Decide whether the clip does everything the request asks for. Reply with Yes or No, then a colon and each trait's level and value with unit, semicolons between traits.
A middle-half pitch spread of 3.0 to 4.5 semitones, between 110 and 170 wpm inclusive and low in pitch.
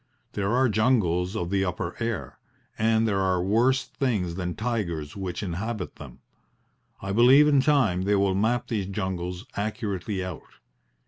Yes: average, 3.9 semitones; average, 150 wpm; low, 100 Hz